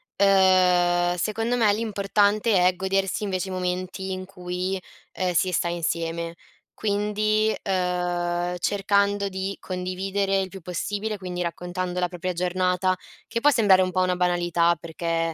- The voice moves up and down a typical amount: No, narrow, 1.9 semitones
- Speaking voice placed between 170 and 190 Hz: Yes, medium, 185 Hz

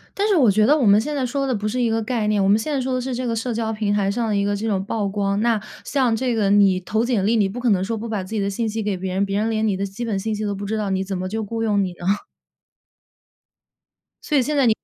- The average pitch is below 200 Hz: No, high, 215 Hz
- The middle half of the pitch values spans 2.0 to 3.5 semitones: Yes, average, 2.9 semitones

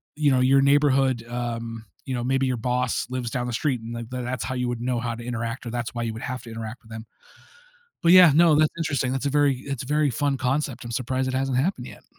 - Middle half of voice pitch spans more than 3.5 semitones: No, narrow, 2.5 semitones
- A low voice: Yes, low, 125 Hz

